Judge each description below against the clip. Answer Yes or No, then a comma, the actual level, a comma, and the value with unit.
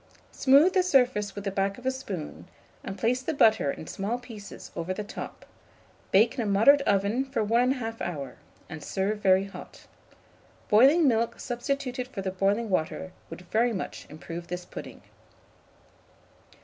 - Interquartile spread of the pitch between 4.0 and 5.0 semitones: Yes, average, 4.7 semitones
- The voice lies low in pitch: No, high, 215 Hz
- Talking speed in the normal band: Yes, average, 160 wpm